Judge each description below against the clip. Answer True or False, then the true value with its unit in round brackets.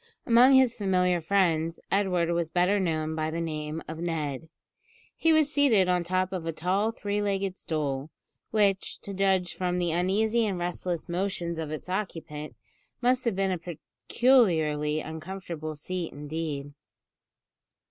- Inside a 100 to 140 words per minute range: False (150 wpm)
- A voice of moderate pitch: True (180 Hz)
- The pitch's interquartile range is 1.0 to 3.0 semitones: False (3.6 semitones)